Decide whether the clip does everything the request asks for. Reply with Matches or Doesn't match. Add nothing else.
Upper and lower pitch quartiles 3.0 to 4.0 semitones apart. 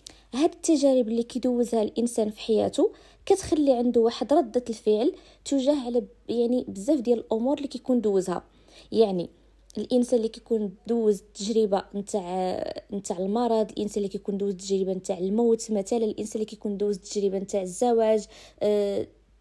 Matches